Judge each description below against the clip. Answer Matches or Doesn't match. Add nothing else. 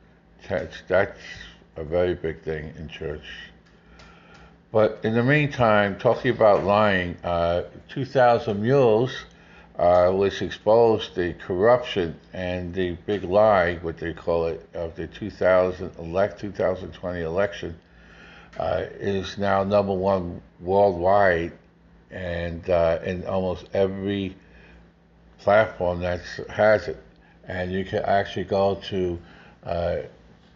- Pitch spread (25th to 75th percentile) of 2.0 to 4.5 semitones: Matches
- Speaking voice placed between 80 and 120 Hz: Matches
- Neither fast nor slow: Doesn't match